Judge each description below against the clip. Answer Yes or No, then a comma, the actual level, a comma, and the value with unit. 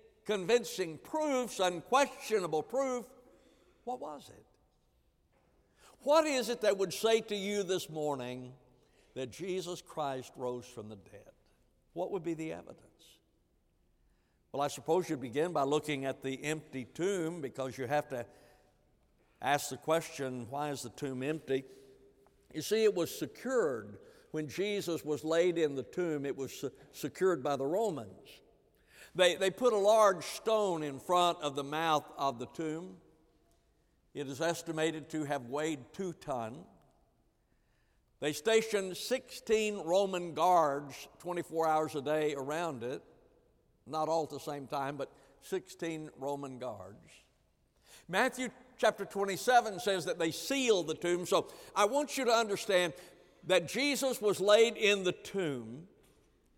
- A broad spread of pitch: Yes, wide, 6.2 semitones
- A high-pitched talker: No, medium, 165 Hz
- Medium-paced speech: Yes, average, 145 wpm